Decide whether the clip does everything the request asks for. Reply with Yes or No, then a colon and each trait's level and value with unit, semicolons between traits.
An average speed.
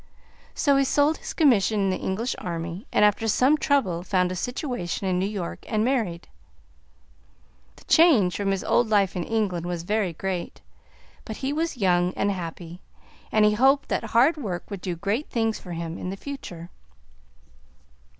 Yes: average, 175 wpm